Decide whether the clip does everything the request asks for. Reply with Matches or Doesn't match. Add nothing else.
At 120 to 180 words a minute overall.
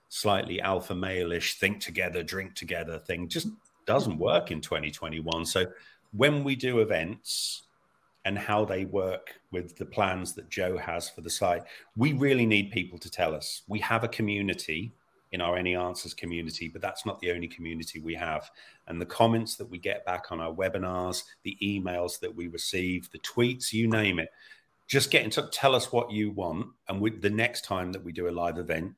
Doesn't match